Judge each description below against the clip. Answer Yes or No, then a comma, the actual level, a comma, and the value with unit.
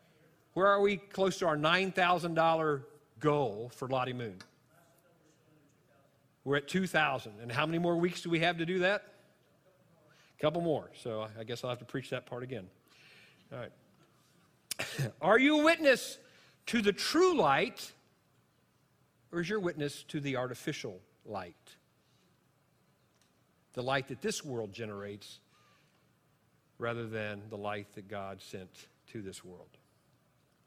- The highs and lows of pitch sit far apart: Yes, wide, 6.0 semitones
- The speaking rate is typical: Yes, average, 145 wpm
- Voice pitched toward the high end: No, medium, 150 Hz